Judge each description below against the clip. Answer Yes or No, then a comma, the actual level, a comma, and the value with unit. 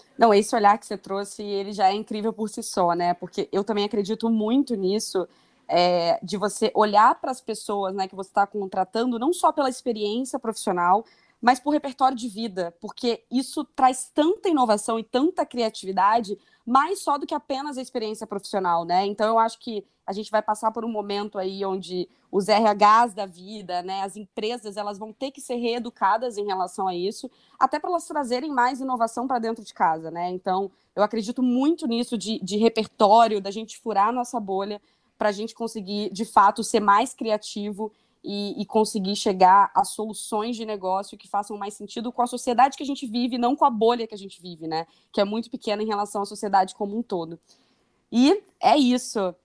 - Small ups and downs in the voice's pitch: No, average, 3.4 semitones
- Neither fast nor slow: No, fast, 200 wpm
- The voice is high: Yes, high, 215 Hz